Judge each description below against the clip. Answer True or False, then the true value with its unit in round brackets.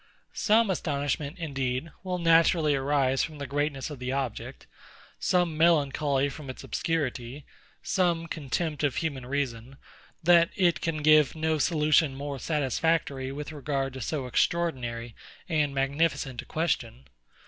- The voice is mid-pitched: True (145 Hz)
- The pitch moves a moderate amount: True (3.4 semitones)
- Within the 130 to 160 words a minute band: True (135 wpm)